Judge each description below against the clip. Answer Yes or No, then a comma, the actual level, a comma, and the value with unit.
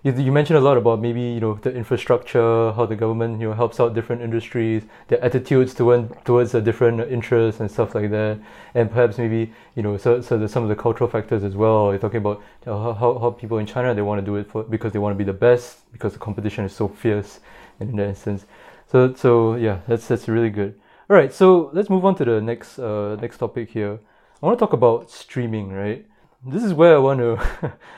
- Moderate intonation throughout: No, narrow, 2.3 semitones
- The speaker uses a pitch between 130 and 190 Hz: No, low, 115 Hz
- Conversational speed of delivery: No, fast, 230 wpm